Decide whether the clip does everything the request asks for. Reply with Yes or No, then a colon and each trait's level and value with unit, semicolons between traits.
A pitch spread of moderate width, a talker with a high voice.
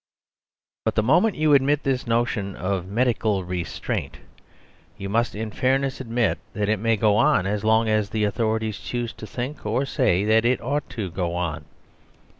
No: average, 3.7 semitones; low, 110 Hz